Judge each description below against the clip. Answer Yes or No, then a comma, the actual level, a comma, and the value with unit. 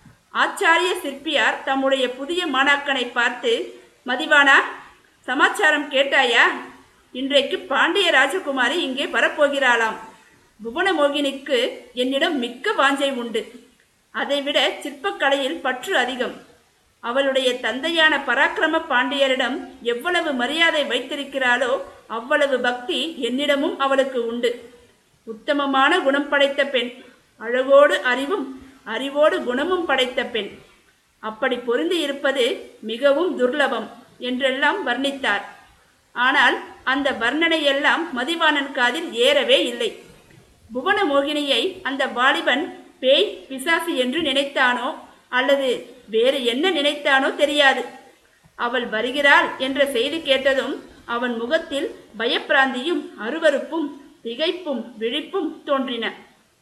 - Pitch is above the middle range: Yes, very high, 275 Hz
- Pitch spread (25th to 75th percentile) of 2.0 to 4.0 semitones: Yes, average, 3.5 semitones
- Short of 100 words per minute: Yes, average, 85 wpm